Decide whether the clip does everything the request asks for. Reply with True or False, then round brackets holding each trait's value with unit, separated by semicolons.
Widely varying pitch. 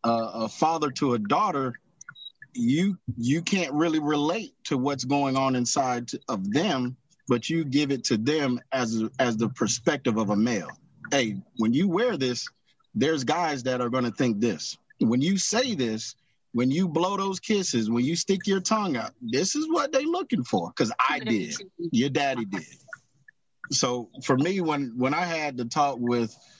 True (6.7 semitones)